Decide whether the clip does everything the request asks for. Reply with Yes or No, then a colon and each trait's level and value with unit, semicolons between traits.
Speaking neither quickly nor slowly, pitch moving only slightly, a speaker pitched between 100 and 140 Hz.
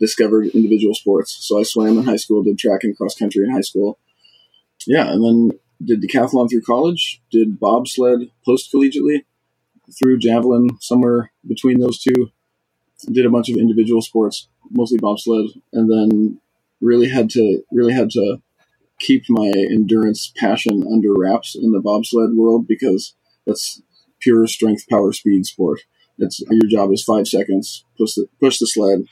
Yes: average, 160 wpm; narrow, 2.3 semitones; low, 115 Hz